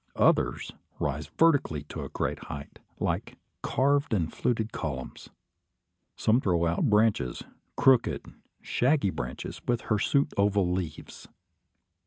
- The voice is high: No, low, 100 Hz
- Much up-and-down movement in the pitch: Yes, wide, 7.4 semitones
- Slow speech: Yes, slow, 115 wpm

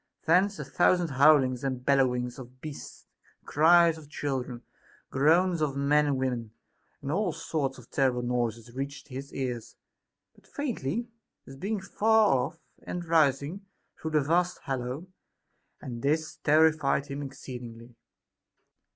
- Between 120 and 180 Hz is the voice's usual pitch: Yes, medium, 140 Hz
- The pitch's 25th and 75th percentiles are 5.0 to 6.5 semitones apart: No, average, 3.8 semitones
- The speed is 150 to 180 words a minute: No, average, 140 wpm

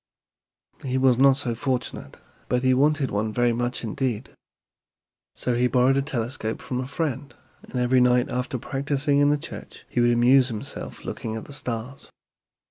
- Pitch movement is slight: Yes, narrow, 2.1 semitones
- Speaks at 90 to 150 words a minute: No, average, 170 wpm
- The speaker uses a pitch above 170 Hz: No, low, 125 Hz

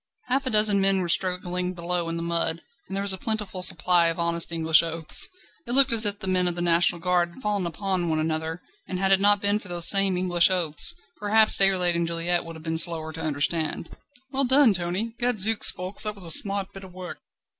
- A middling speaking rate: No, fast, 230 wpm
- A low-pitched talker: No, medium, 180 Hz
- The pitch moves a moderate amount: Yes, average, 3.0 semitones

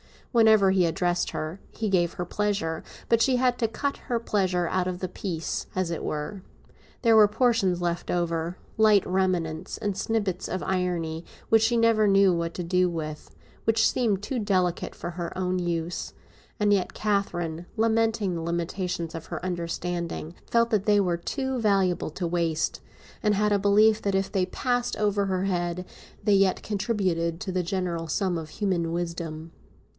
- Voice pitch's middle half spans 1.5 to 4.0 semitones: Yes, average, 3.4 semitones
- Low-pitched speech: No, medium, 185 Hz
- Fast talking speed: No, average, 175 wpm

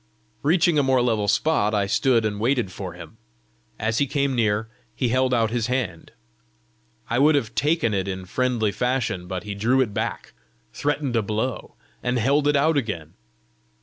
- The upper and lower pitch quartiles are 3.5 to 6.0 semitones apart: Yes, average, 4.2 semitones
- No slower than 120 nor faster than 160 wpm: No, average, 180 wpm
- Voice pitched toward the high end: No, low, 120 Hz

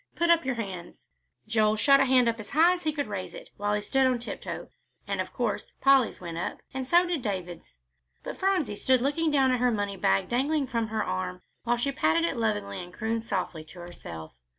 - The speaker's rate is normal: No, fast, 220 wpm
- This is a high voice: Yes, high, 230 Hz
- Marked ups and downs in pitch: Yes, wide, 6.2 semitones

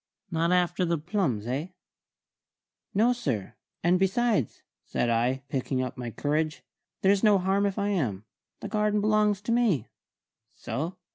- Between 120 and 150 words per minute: Yes, average, 145 wpm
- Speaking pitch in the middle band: Yes, medium, 175 Hz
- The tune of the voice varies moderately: No, wide, 7.4 semitones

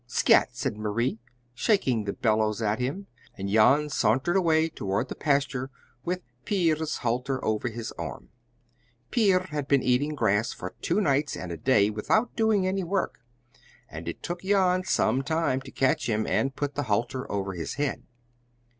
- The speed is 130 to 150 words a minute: No, average, 165 wpm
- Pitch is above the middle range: No, low, 135 Hz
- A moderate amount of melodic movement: No, wide, 6.9 semitones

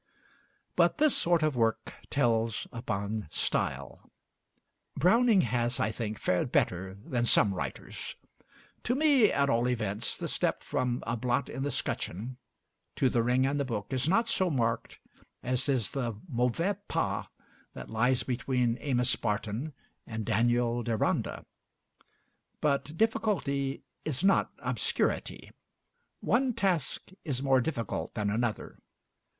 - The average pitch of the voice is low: Yes, low, 125 Hz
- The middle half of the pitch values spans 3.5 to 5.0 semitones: Yes, average, 4.1 semitones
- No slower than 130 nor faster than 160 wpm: Yes, slow, 135 wpm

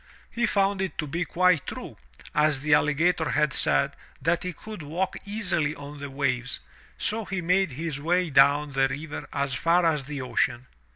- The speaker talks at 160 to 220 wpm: Yes, average, 180 wpm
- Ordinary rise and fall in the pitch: Yes, average, 4.1 semitones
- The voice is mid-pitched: Yes, medium, 155 Hz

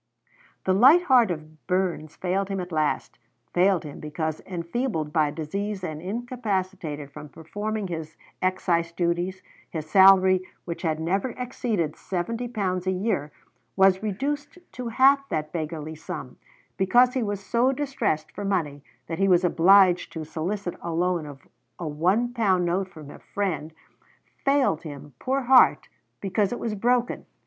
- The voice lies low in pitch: No, medium, 185 Hz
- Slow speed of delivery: No, average, 155 wpm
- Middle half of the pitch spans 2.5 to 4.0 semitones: No, average, 5.1 semitones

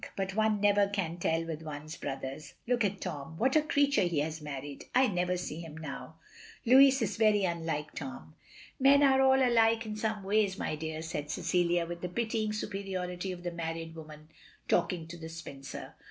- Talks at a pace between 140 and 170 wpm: No, average, 190 wpm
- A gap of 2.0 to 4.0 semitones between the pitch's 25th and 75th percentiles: No, average, 5.1 semitones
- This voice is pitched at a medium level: Yes, medium, 175 Hz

